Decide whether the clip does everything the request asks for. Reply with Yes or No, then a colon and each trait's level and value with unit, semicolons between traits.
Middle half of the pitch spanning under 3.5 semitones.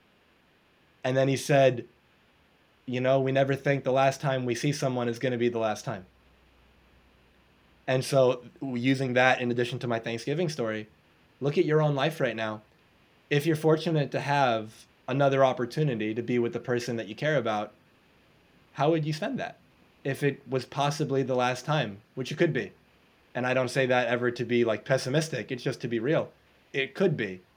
Yes: average, 2.8 semitones